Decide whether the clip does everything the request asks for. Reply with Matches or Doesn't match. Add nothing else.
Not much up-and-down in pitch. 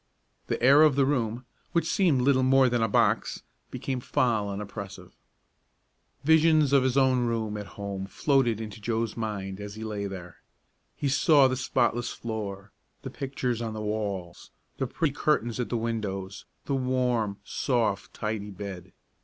Doesn't match